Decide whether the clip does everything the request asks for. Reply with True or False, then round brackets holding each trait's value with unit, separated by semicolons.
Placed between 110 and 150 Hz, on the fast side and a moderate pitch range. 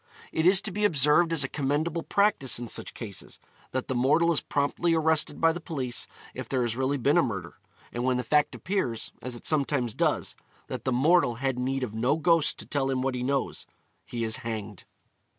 True (135 Hz; 210 wpm; 4.5 semitones)